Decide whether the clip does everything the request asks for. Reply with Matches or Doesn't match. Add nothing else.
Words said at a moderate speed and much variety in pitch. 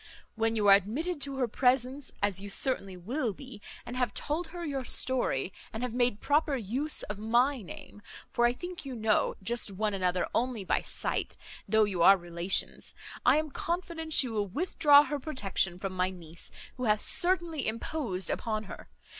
Matches